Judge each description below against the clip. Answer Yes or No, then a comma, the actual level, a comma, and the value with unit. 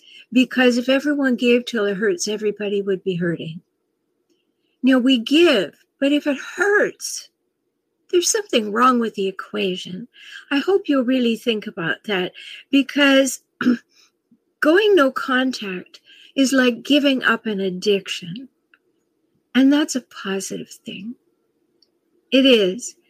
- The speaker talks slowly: Yes, slow, 125 wpm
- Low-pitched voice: No, very high, 265 Hz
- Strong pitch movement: Yes, wide, 8.1 semitones